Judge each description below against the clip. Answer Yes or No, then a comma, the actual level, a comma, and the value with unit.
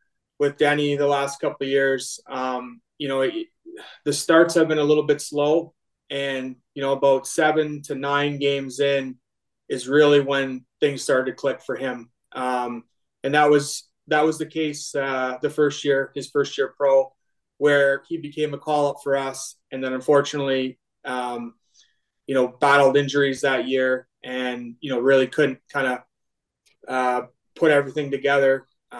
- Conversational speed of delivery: Yes, average, 170 wpm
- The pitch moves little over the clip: Yes, narrow, 2.1 semitones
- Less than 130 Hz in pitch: No, medium, 140 Hz